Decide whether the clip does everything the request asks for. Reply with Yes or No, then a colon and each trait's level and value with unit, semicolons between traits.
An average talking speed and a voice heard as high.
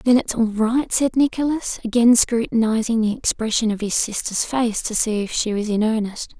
Yes: average, 195 wpm; high, 225 Hz